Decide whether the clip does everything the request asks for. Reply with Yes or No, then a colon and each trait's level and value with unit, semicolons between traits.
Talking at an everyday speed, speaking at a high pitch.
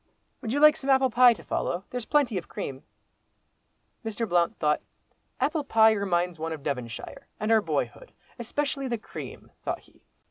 Yes: average, 165 wpm; high, 225 Hz